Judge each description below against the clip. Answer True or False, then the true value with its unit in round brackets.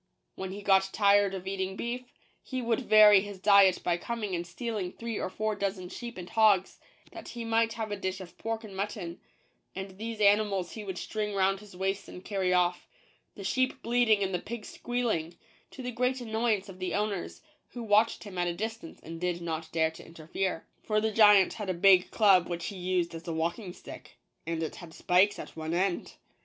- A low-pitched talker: False (195 Hz)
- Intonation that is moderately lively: True (3.3 semitones)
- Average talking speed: False (215 wpm)